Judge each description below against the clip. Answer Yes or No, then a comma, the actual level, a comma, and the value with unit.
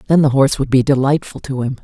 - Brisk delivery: Yes, fast, 260 wpm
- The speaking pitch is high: No, low, 135 Hz